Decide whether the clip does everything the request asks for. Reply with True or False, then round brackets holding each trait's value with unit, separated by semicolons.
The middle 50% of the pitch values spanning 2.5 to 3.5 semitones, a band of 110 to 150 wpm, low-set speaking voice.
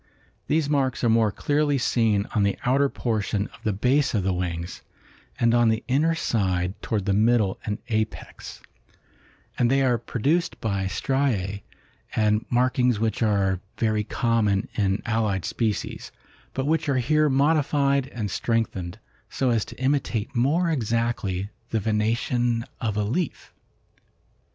False (4.3 semitones; 145 wpm; 115 Hz)